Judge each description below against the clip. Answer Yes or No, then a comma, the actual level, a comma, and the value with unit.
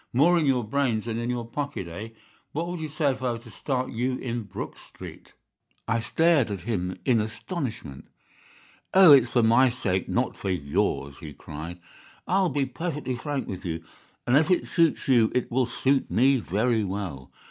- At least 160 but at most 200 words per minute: Yes, average, 190 wpm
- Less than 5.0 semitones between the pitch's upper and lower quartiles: No, average, 5.3 semitones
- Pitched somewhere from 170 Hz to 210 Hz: No, low, 120 Hz